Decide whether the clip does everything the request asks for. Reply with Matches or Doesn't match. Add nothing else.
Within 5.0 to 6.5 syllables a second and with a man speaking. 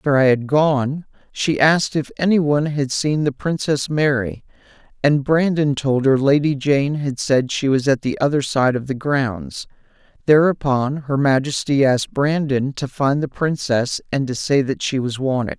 Doesn't match